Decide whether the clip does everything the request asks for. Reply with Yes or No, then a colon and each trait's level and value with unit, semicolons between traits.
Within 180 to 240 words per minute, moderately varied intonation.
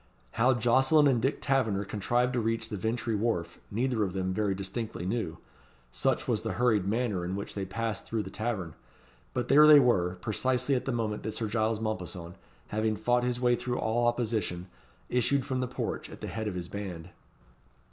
Yes: average, 195 wpm; average, 3.8 semitones